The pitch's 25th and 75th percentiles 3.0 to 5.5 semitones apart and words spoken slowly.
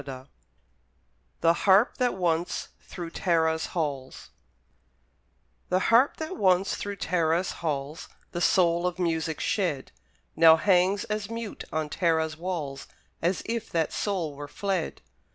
Yes: average, 3.3 semitones; slow, 130 wpm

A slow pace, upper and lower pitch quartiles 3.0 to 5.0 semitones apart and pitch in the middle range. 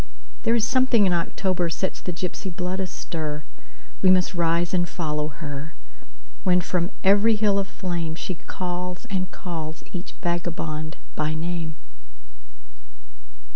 No: slow, 120 wpm; narrow, 2.6 semitones; medium, 175 Hz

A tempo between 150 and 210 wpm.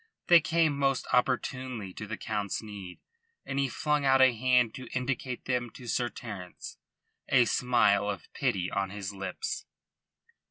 Yes: average, 155 wpm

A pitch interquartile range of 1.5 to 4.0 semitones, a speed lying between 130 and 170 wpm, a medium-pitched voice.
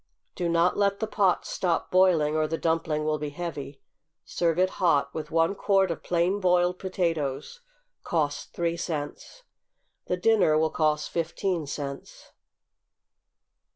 Yes: average, 3.1 semitones; average, 140 wpm; medium, 170 Hz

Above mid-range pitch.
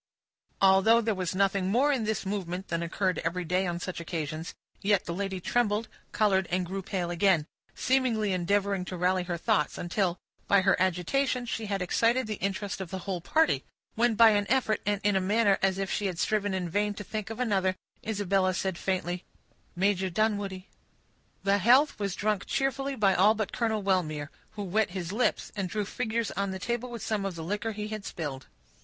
Yes: high, 195 Hz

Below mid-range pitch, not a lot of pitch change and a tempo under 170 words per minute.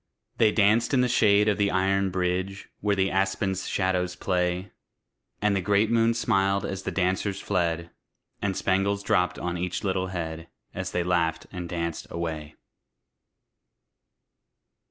Yes: very low, 95 Hz; narrow, 2.1 semitones; average, 145 wpm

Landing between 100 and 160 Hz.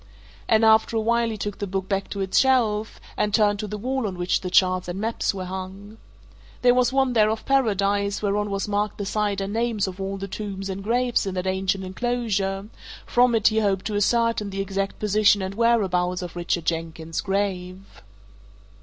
No: high, 200 Hz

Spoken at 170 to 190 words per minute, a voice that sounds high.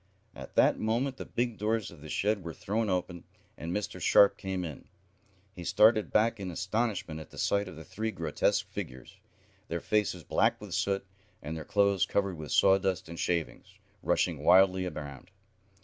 No: average, 180 wpm; very low, 95 Hz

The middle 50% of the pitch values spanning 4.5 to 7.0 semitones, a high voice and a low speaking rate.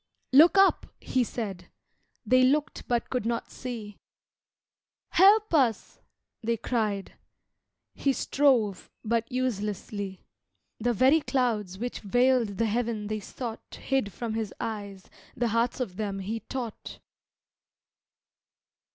No: average, 3.6 semitones; high, 230 Hz; slow, 115 wpm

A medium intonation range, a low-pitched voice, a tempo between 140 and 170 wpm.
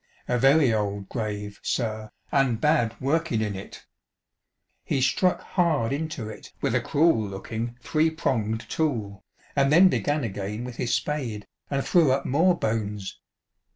No: wide, 5.7 semitones; low, 120 Hz; average, 150 wpm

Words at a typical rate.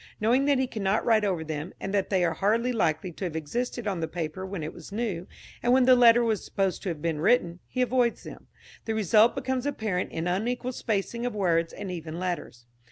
No: fast, 220 wpm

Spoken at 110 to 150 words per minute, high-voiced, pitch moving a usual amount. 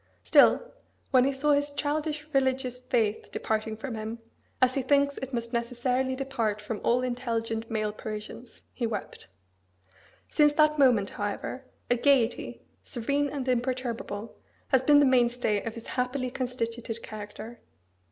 Yes: average, 140 wpm; very high, 250 Hz; average, 3.0 semitones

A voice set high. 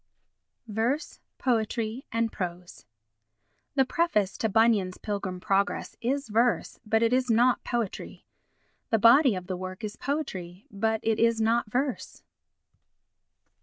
Yes: high, 225 Hz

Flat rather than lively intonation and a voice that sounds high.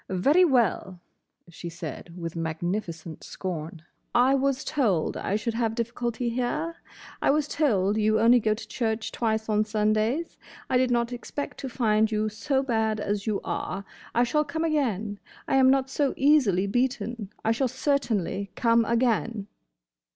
No: average, 4.1 semitones; high, 225 Hz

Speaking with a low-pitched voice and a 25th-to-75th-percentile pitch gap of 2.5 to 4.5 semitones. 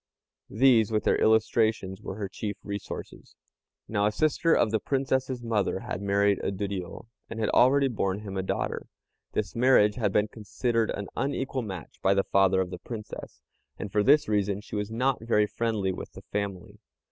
Yes: low, 105 Hz; average, 2.8 semitones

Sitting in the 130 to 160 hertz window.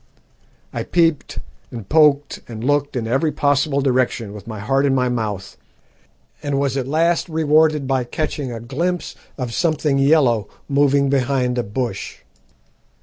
Yes: low, 135 Hz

